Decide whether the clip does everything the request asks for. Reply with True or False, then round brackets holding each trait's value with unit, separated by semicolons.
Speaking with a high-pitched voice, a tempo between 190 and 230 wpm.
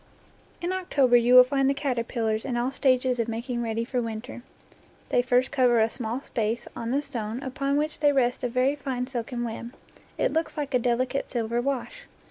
True (250 Hz; 200 wpm)